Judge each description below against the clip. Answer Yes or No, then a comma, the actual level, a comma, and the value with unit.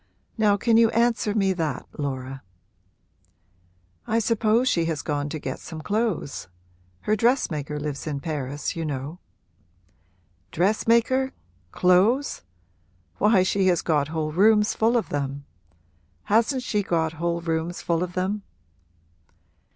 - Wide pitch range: Yes, wide, 6.2 semitones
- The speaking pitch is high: No, medium, 180 Hz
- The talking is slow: Yes, slow, 130 wpm